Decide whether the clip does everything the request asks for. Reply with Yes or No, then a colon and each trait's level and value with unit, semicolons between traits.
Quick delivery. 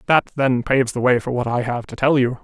Yes: fast, 295 wpm